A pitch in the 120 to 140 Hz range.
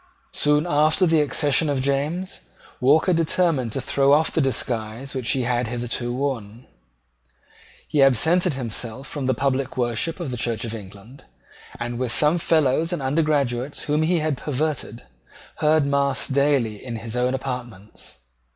Yes: low, 135 Hz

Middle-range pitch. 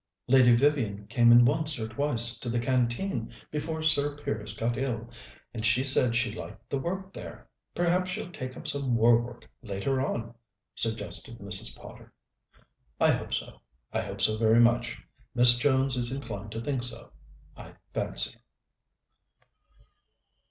No: low, 120 Hz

